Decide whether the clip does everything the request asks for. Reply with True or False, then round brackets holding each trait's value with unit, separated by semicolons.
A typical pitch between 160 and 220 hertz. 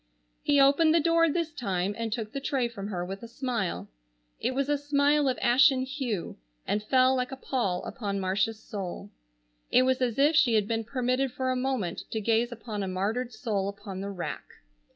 False (240 Hz)